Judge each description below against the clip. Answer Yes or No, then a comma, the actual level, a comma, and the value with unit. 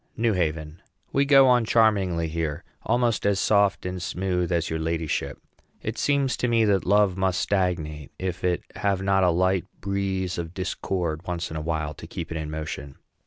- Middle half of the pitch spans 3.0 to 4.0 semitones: Yes, average, 3.5 semitones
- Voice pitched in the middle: No, very low, 90 Hz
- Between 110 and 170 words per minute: No, average, 185 wpm